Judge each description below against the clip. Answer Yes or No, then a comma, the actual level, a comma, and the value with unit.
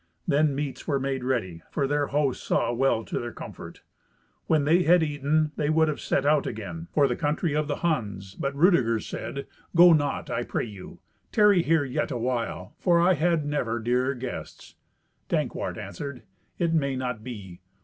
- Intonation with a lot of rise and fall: No, average, 4.2 semitones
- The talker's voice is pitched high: No, medium, 140 Hz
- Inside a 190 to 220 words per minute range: No, average, 180 wpm